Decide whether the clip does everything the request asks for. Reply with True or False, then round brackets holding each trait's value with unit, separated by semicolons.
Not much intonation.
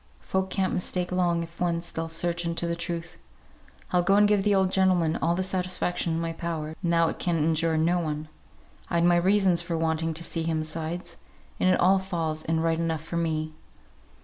True (1.7 semitones)